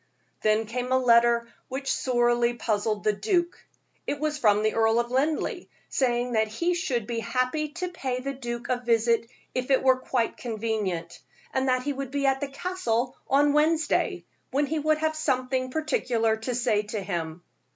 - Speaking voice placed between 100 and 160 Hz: No, very high, 250 Hz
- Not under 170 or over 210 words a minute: Yes, average, 180 wpm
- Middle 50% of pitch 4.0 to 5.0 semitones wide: No, average, 3.6 semitones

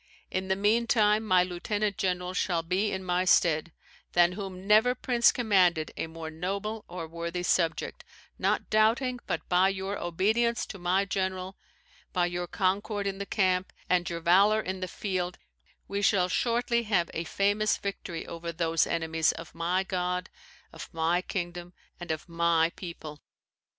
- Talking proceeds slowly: No, average, 160 wpm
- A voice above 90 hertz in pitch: Yes, medium, 185 Hz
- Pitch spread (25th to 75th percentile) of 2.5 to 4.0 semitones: Yes, average, 2.8 semitones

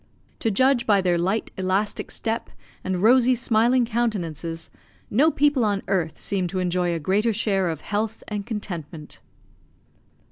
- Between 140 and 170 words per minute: Yes, average, 145 wpm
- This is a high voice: Yes, high, 200 Hz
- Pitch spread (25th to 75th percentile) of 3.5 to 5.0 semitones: Yes, average, 4.3 semitones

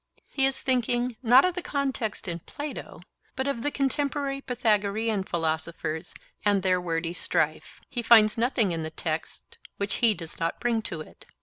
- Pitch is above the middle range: Yes, high, 220 Hz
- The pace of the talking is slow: No, average, 170 wpm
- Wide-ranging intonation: Yes, wide, 7.1 semitones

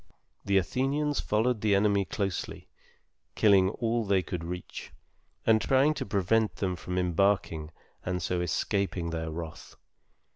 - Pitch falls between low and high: No, low, 100 Hz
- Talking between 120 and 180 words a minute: Yes, slow, 135 wpm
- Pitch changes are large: No, average, 3.7 semitones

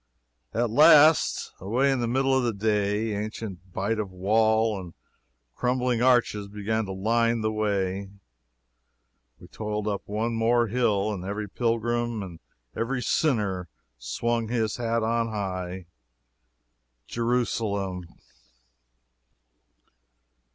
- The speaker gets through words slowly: Yes, slow, 115 wpm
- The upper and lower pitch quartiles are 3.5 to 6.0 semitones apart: No, average, 2.9 semitones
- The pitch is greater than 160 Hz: No, low, 110 Hz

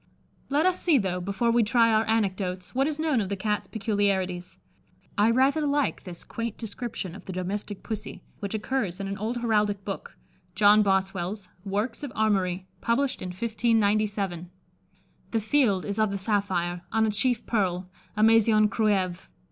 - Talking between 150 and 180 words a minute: Yes, average, 170 wpm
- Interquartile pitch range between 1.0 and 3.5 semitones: Yes, average, 3.1 semitones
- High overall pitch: Yes, high, 210 Hz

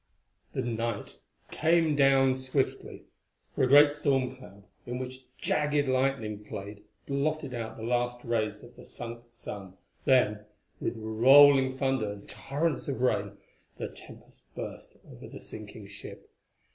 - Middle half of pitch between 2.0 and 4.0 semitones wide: Yes, average, 3.6 semitones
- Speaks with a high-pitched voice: No, low, 130 Hz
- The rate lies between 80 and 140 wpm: Yes, slow, 135 wpm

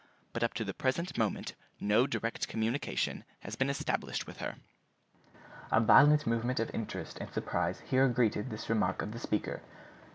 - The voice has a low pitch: Yes, low, 115 Hz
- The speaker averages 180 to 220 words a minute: No, average, 165 wpm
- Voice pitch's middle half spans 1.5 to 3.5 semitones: Yes, average, 2.9 semitones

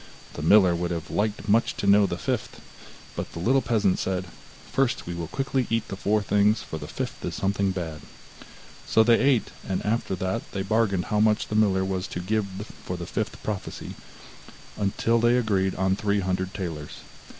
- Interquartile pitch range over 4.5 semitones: No, average, 2.9 semitones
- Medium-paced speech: Yes, average, 190 wpm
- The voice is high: No, low, 100 Hz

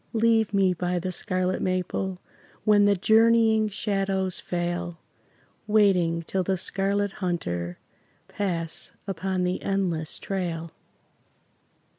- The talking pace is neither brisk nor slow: No, slow, 105 wpm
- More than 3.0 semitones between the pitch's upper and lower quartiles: No, narrow, 2.5 semitones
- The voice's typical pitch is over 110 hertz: Yes, high, 190 Hz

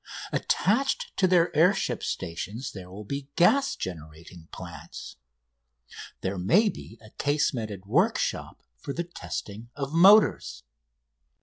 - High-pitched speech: No, low, 130 Hz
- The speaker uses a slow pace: Yes, slow, 120 wpm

